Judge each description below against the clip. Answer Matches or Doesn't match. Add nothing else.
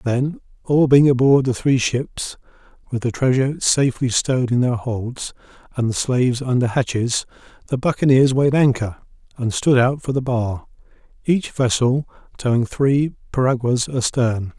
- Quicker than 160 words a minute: Doesn't match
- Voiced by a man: Matches